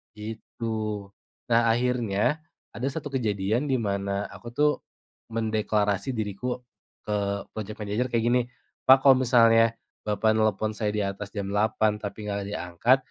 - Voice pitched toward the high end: No, low, 110 Hz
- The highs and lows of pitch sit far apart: No, average, 2.9 semitones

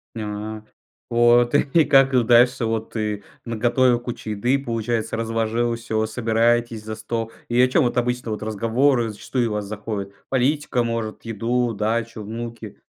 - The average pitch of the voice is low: Yes, low, 115 Hz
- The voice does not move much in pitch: Yes, narrow, 1.8 semitones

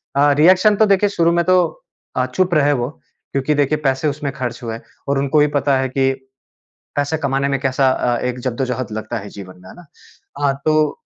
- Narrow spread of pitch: No, average, 3.1 semitones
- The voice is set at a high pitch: No, medium, 140 Hz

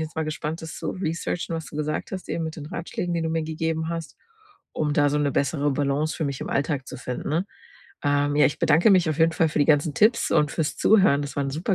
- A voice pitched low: No, medium, 155 Hz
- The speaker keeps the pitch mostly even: Yes, narrow, 2.2 semitones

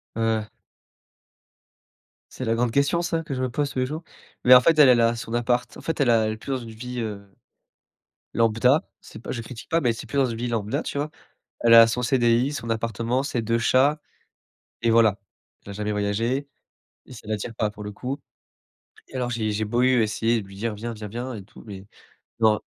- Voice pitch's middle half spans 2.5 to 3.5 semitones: Yes, average, 2.8 semitones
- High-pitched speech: No, low, 115 Hz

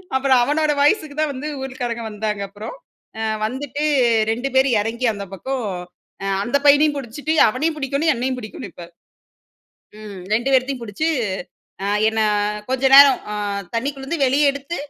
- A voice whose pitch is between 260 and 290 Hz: Yes, very high, 265 Hz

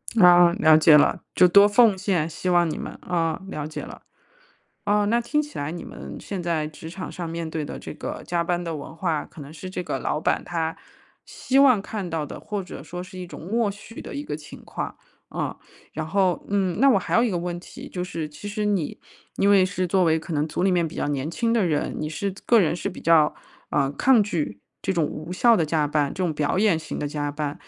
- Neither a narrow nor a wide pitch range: Yes, average, 4.2 semitones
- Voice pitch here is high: No, medium, 175 Hz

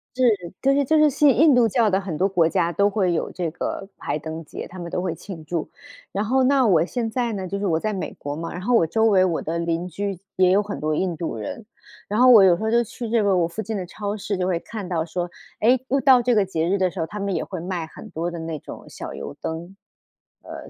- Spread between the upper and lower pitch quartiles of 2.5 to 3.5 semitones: No, average, 4.5 semitones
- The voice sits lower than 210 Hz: Yes, high, 190 Hz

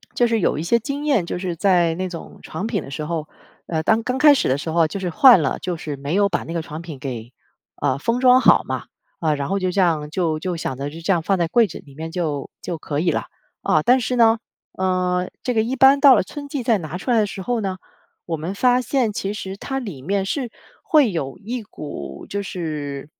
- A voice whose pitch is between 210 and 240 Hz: No, medium, 185 Hz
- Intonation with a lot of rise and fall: Yes, wide, 6.4 semitones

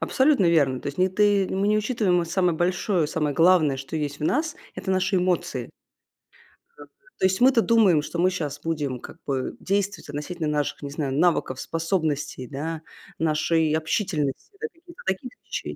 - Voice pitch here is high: No, medium, 170 Hz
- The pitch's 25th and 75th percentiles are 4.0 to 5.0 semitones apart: Yes, average, 4.4 semitones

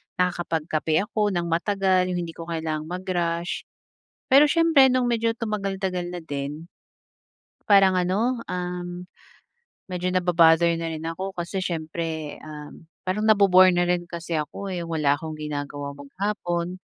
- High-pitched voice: No, medium, 175 Hz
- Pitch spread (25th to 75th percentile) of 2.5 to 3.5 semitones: Yes, average, 2.9 semitones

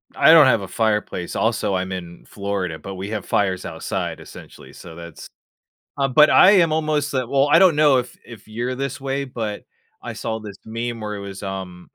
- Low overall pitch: Yes, low, 110 Hz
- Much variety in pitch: Yes, wide, 6.0 semitones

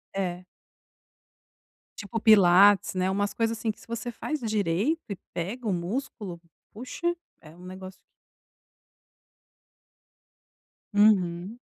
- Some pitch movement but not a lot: Yes, average, 3.8 semitones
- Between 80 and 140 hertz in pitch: No, high, 205 Hz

